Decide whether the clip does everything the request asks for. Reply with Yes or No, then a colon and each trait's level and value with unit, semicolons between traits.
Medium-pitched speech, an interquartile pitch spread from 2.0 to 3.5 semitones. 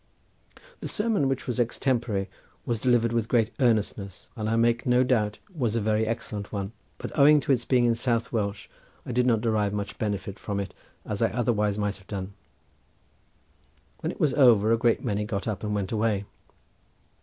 No: low, 115 Hz; average, 2.8 semitones